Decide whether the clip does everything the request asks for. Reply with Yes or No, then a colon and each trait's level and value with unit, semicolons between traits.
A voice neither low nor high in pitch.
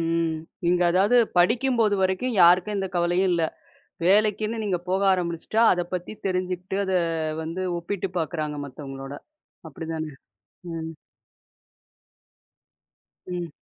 Yes: medium, 180 Hz